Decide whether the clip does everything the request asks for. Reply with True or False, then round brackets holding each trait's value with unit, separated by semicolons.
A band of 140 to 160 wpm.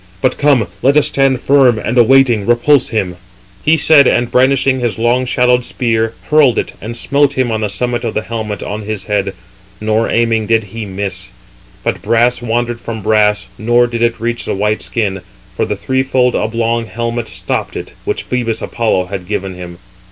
False (185 wpm)